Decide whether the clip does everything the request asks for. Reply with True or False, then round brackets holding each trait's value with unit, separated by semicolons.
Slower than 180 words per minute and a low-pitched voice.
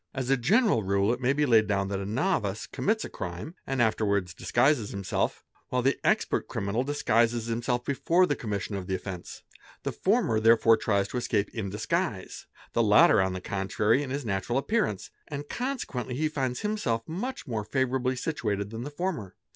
False (185 wpm; 115 Hz)